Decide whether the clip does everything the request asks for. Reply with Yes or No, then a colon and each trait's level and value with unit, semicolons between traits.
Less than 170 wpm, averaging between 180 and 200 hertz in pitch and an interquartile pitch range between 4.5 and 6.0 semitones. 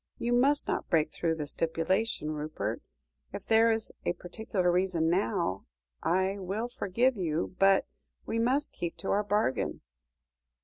Yes: average, 145 wpm; high, 190 Hz; average, 5.1 semitones